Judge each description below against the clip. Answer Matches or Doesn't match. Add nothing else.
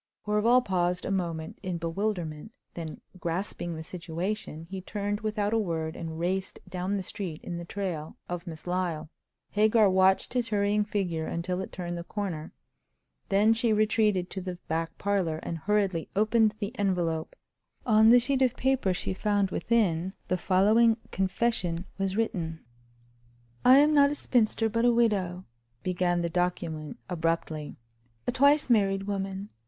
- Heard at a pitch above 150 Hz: Matches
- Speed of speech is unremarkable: Matches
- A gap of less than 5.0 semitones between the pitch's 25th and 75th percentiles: Matches